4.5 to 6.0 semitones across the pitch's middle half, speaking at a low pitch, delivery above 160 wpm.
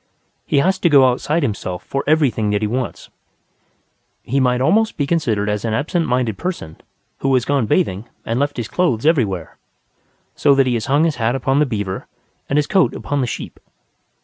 Yes: average, 4.9 semitones; low, 130 Hz; average, 195 wpm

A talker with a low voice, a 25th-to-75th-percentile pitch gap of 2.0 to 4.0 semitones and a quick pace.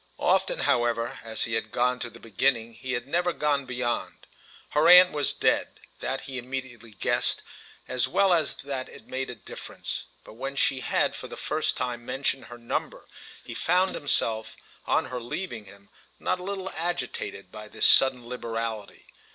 No: low, 125 Hz; average, 3.6 semitones; average, 170 wpm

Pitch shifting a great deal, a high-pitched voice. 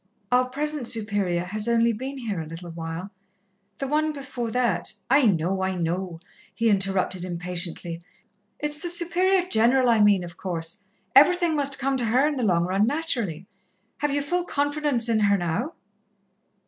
Yes: wide, 7.6 semitones; high, 230 Hz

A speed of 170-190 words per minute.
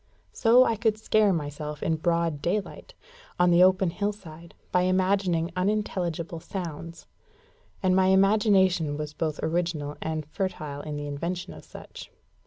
No: average, 140 wpm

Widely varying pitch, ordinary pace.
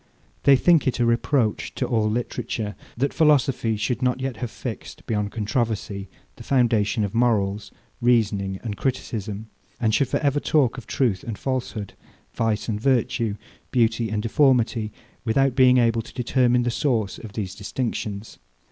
No: average, 3.0 semitones; average, 155 wpm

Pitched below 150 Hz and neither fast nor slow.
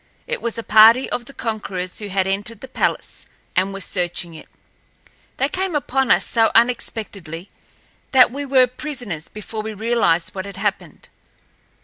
No: high, 220 Hz; average, 160 wpm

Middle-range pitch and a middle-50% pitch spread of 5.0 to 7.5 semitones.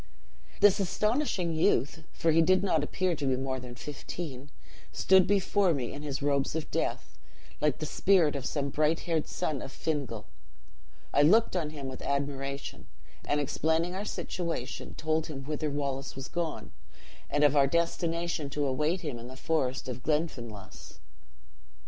No: medium, 150 Hz; average, 3.5 semitones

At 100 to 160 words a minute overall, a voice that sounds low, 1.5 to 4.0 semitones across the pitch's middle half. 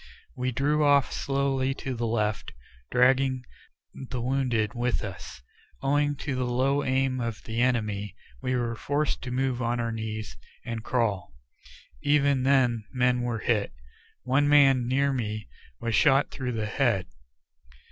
Yes: average, 145 wpm; low, 125 Hz; average, 2.8 semitones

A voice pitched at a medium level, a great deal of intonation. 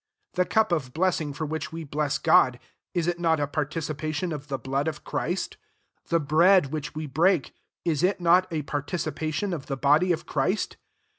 No: medium, 155 Hz; average, 3.1 semitones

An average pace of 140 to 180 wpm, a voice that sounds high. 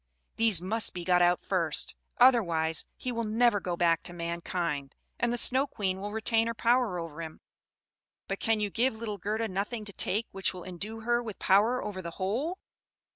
No: average, 190 wpm; high, 205 Hz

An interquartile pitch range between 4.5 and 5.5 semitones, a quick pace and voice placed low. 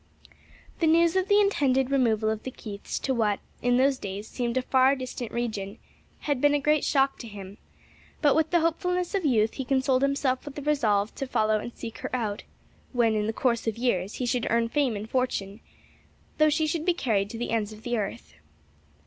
No: average, 4.8 semitones; fast, 210 wpm; very high, 250 Hz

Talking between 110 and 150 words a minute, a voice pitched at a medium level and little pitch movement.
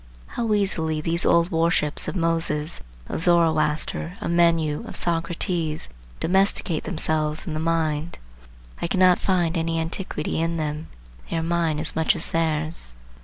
Yes: average, 145 wpm; medium, 165 Hz; narrow, 1.6 semitones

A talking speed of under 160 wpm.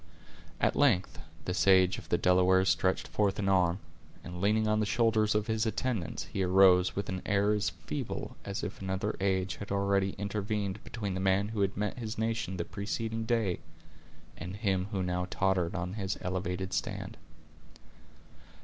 No: average, 170 wpm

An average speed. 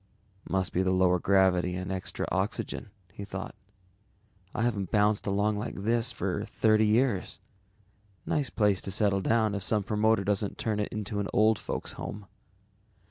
Yes: average, 160 wpm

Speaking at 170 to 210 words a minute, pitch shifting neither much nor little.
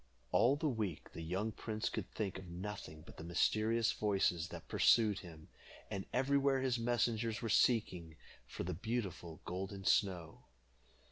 No: average, 150 wpm; average, 4.6 semitones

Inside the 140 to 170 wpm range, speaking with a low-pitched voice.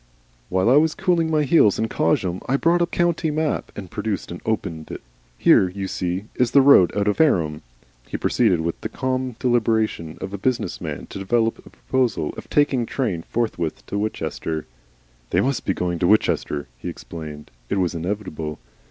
No: average, 185 wpm; low, 105 Hz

